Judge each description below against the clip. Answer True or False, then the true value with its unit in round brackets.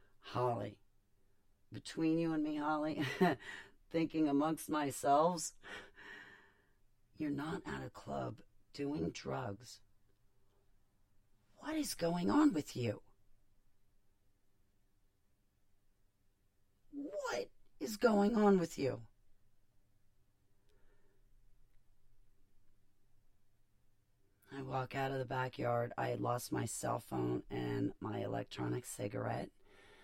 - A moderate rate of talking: False (90 wpm)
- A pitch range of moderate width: True (4.9 semitones)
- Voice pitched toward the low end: True (100 Hz)